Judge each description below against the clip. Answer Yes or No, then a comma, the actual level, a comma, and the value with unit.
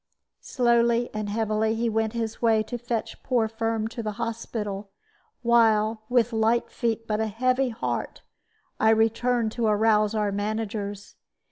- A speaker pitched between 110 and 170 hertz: No, high, 225 Hz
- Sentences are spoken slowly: No, average, 145 wpm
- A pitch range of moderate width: No, narrow, 1.5 semitones